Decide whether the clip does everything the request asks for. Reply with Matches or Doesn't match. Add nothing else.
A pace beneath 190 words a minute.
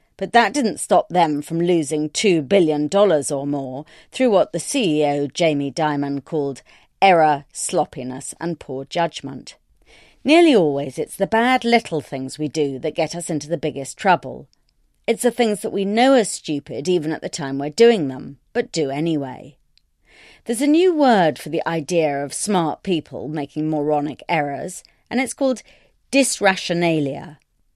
Matches